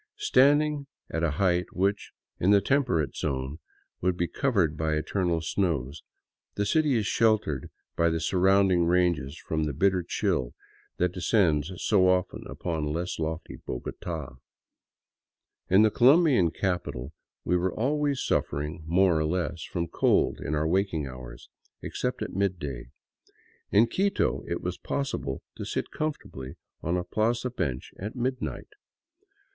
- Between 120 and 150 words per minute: Yes, average, 140 wpm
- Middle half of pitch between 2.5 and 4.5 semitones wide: No, average, 5.0 semitones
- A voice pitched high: No, very low, 90 Hz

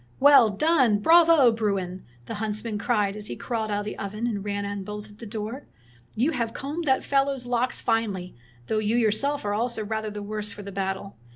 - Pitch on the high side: Yes, high, 215 Hz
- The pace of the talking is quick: Yes, fast, 215 wpm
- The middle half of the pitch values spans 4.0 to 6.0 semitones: No, average, 3.1 semitones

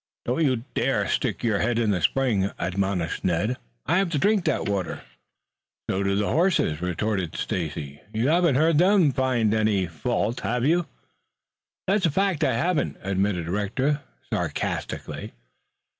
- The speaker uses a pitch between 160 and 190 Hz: No, low, 115 Hz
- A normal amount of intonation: No, wide, 7.6 semitones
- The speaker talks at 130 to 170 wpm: Yes, average, 150 wpm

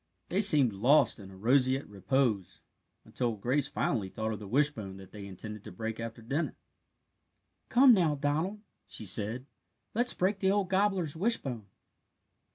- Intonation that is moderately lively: No, wide, 8.0 semitones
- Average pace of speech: Yes, average, 155 wpm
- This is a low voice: Yes, low, 130 Hz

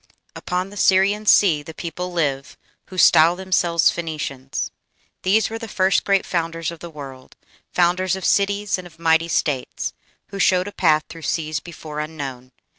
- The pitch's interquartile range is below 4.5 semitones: Yes, average, 3.4 semitones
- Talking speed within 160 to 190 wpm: Yes, average, 165 wpm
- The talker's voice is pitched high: No, medium, 170 Hz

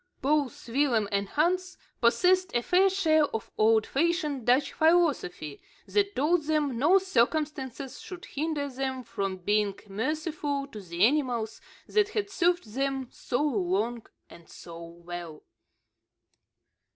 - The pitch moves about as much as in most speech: No, wide, 6.5 semitones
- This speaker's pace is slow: Yes, slow, 125 wpm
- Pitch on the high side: Yes, very high, 270 Hz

